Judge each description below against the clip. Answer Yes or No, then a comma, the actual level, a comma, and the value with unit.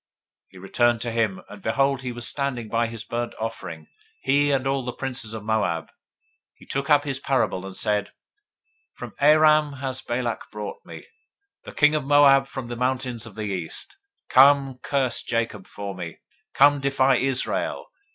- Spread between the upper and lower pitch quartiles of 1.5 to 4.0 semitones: Yes, average, 3.5 semitones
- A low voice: Yes, low, 125 Hz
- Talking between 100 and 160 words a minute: No, average, 170 wpm